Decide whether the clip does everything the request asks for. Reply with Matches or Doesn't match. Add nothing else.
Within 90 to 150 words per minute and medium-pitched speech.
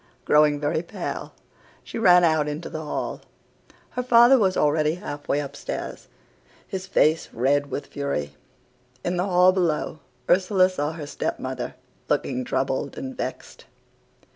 Matches